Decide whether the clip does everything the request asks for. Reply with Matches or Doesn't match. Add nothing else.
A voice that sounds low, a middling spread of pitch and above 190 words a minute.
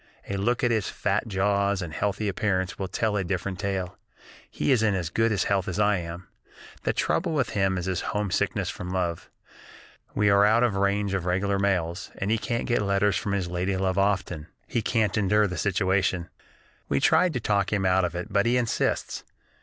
Doesn't match